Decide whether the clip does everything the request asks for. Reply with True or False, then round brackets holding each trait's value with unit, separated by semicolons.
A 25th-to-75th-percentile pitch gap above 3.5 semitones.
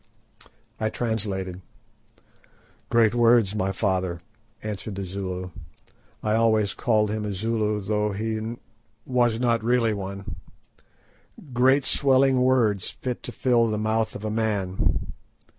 False (3.0 semitones)